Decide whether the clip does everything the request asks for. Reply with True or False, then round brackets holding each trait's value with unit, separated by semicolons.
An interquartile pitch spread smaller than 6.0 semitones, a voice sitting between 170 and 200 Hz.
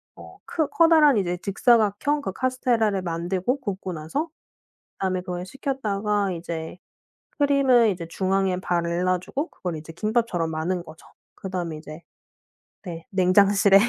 True (5.2 semitones; 190 Hz)